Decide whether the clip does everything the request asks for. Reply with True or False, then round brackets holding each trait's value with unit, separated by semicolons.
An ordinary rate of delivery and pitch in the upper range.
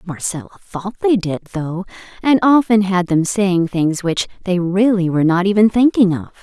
True (180 wpm; 195 Hz)